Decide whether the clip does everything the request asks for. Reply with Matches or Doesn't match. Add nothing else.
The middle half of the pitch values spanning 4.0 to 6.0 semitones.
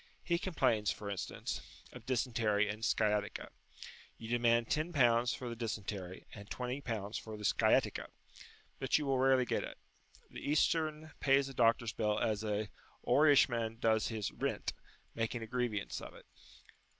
Doesn't match